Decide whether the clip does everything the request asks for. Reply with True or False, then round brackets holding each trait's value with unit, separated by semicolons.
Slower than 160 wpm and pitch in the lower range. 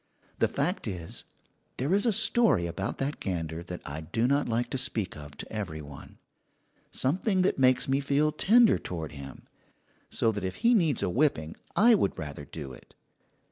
False (180 wpm; 115 Hz)